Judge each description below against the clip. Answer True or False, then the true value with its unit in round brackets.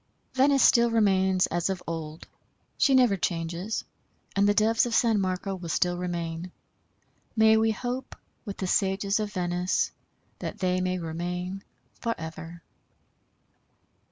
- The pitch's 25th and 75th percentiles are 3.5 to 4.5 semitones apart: True (3.8 semitones)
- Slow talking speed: True (130 wpm)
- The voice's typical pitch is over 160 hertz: True (190 Hz)